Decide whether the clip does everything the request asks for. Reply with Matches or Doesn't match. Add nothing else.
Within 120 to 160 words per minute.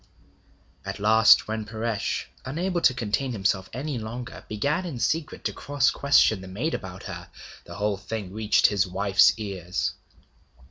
Matches